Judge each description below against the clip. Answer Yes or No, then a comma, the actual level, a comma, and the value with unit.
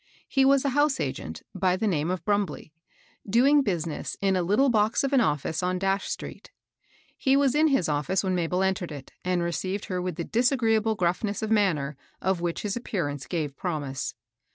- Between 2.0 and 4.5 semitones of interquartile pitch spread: No, average, 4.9 semitones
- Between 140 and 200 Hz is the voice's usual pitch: Yes, high, 190 Hz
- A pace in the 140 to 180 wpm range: No, average, 190 wpm